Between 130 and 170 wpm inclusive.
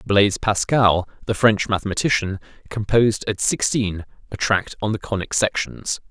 Yes: average, 140 wpm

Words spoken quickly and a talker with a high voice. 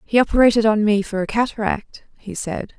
No: average, 195 wpm; high, 215 Hz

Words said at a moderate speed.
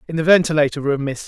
No: fast, 235 wpm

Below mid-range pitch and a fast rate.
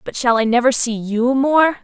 No: very high, 250 Hz; fast, 230 wpm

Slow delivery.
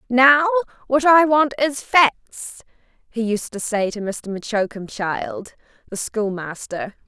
Yes: slow, 125 wpm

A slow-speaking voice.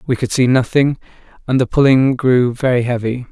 No: average, 180 wpm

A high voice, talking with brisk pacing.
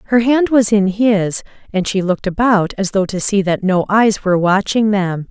Yes: high, 200 Hz; fast, 215 wpm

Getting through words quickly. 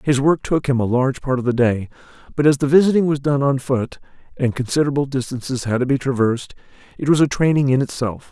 Yes: fast, 225 wpm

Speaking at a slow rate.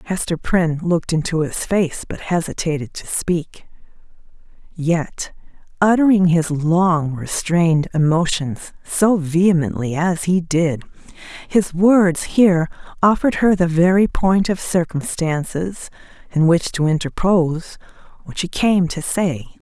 Yes: slow, 120 wpm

